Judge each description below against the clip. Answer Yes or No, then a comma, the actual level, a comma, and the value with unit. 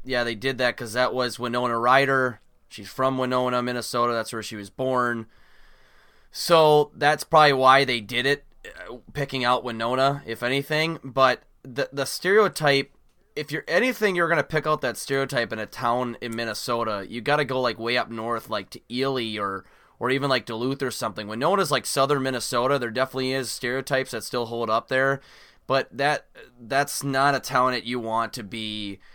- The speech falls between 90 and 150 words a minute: No, average, 190 wpm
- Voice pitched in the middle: No, low, 125 Hz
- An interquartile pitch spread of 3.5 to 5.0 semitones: No, narrow, 2.6 semitones